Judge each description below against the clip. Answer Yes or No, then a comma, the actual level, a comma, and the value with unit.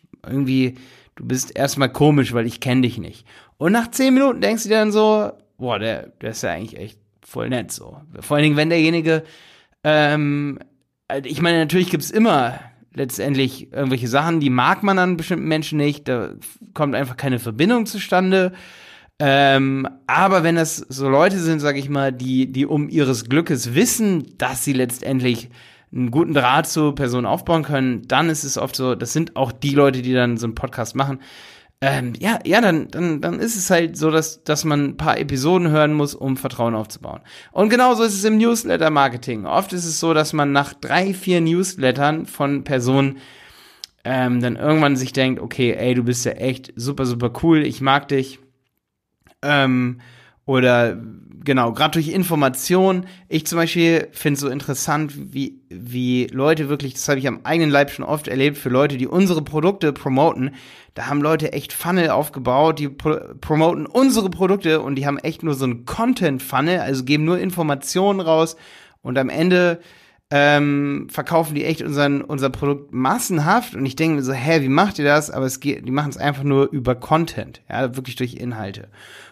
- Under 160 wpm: No, average, 185 wpm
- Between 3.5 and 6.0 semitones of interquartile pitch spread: Yes, average, 3.8 semitones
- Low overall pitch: No, medium, 145 Hz